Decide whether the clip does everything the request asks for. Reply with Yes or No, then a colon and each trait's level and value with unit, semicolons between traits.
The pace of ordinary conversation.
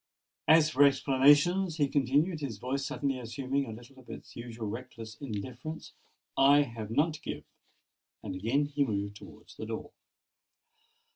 Yes: average, 150 wpm